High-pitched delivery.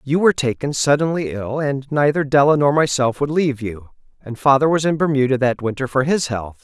No: medium, 140 Hz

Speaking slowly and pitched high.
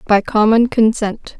Yes: slow, 130 wpm; high, 220 Hz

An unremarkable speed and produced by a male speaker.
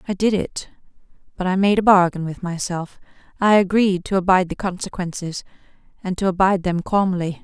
No: average, 160 wpm; female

